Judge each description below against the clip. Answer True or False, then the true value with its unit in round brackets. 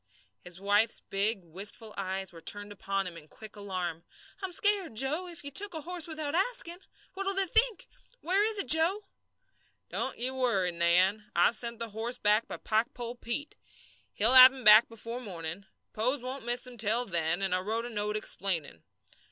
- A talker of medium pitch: False (225 Hz)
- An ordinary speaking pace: True (185 wpm)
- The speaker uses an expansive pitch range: True (6.6 semitones)